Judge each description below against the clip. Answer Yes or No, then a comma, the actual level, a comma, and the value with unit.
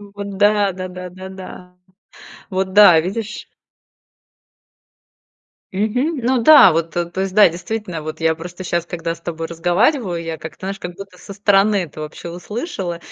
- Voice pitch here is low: No, medium, 185 Hz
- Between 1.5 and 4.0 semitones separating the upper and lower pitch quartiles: Yes, average, 3.1 semitones